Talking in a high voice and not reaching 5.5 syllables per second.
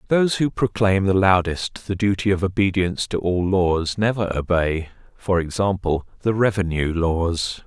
No: very low, 95 Hz; 4.6 syllables/s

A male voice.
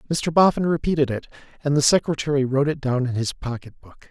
Yes: male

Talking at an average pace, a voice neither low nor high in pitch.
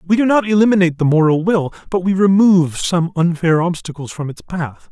Yes: average, 195 wpm; medium, 175 Hz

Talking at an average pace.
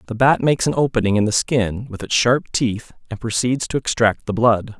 No: fast, 225 wpm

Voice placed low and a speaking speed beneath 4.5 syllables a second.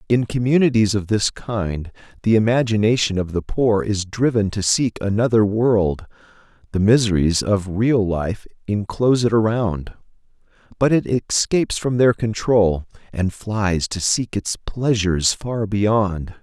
Yes: low, 105 Hz; 4.2 syllables/s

